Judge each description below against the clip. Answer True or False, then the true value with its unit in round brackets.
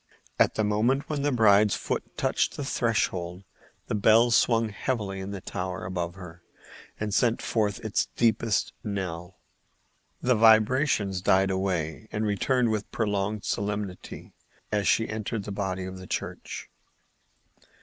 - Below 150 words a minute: True (140 wpm)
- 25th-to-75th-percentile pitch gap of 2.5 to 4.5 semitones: True (2.9 semitones)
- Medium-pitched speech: False (105 Hz)